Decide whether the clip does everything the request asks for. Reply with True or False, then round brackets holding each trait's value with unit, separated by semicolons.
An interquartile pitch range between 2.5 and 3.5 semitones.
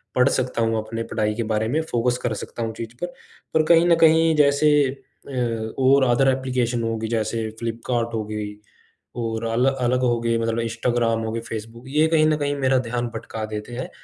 True (2.8 semitones)